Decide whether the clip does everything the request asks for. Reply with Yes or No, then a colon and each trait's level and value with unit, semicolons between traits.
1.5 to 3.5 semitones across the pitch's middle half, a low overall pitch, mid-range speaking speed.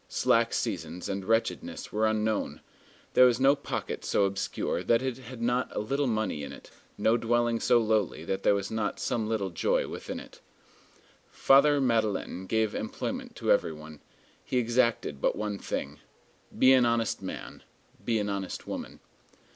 Yes: average, 3.2 semitones; low, 110 Hz; average, 165 wpm